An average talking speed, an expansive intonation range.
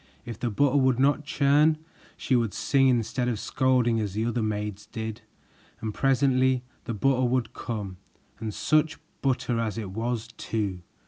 No: average, 165 wpm; average, 3.2 semitones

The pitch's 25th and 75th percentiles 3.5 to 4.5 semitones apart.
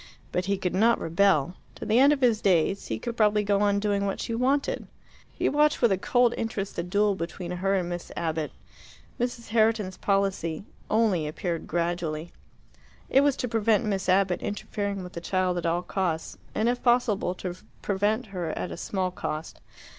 Yes: average, 3.9 semitones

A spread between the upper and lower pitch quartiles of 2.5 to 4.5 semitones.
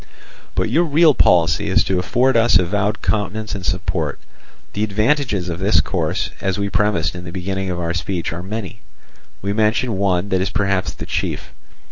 Yes: average, 3.1 semitones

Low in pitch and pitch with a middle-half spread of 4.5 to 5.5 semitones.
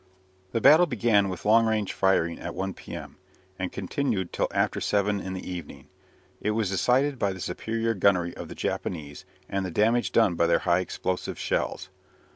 No: very low, 95 Hz; average, 3.9 semitones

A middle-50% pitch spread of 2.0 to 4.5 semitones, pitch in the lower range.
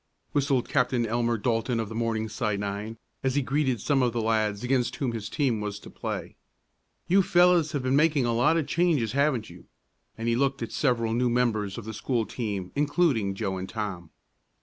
Yes: average, 4.0 semitones; low, 120 Hz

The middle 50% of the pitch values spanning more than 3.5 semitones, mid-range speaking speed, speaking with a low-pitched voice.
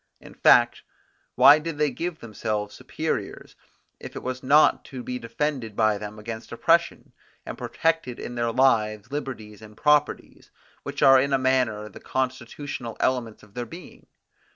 Yes: average, 4.5 semitones; average, 155 wpm; low, 125 Hz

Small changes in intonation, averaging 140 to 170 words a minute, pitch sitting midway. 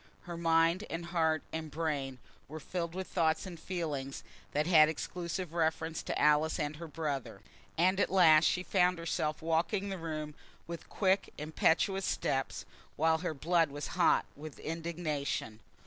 Yes: narrow, 2.2 semitones; average, 155 wpm; medium, 160 Hz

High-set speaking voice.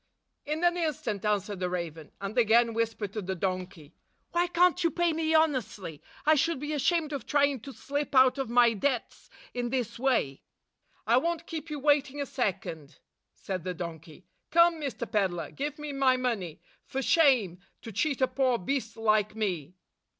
Yes: high, 245 Hz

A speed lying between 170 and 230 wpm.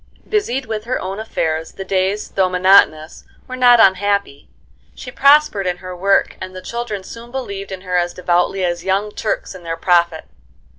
Yes: average, 180 wpm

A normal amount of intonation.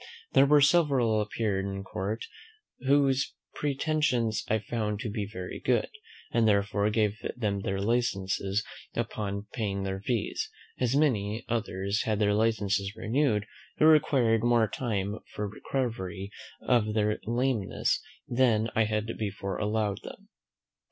Yes: average, 3.0 semitones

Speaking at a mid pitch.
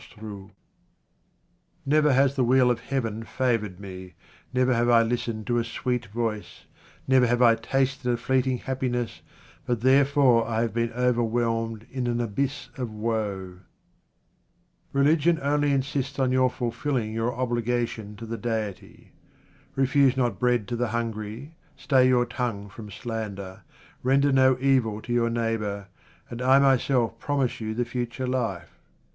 No: low, 120 Hz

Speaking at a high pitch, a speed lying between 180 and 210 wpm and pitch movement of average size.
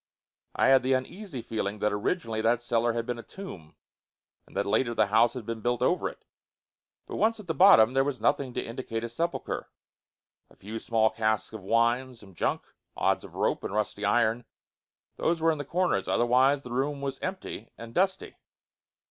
No: low, 120 Hz; average, 190 wpm; average, 4.0 semitones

